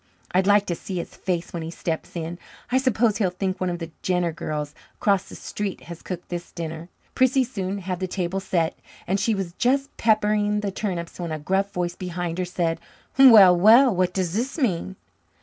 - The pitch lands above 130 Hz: Yes, medium, 185 Hz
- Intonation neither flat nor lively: Yes, average, 3.2 semitones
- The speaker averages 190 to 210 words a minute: Yes, average, 200 wpm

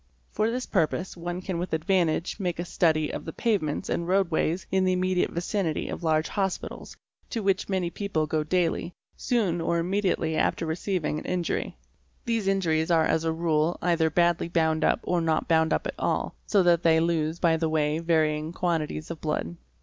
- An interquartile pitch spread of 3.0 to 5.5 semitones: No, narrow, 2.5 semitones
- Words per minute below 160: No, average, 195 wpm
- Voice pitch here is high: No, medium, 170 Hz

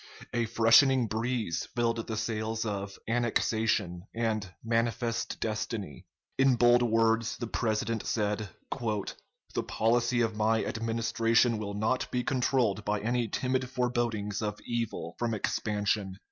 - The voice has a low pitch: Yes, low, 115 Hz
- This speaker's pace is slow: Yes, slow, 125 wpm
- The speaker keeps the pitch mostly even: Yes, narrow, 1.9 semitones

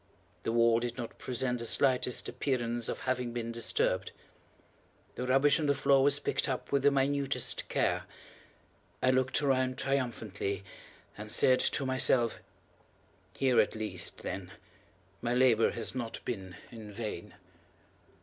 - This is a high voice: No, low, 125 Hz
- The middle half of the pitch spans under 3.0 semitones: Yes, narrow, 2.6 semitones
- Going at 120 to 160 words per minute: Yes, average, 140 wpm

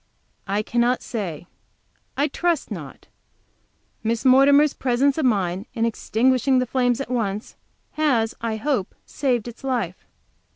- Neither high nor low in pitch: No, high, 245 Hz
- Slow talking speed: Yes, slow, 130 wpm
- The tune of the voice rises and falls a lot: No, average, 3.5 semitones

